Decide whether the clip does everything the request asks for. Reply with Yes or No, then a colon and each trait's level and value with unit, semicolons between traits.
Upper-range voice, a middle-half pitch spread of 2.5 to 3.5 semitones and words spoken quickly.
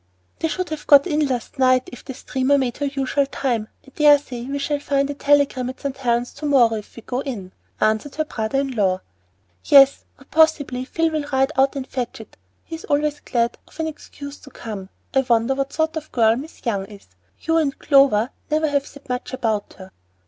Yes: very high, 270 Hz; average, 3.1 semitones; fast, 215 wpm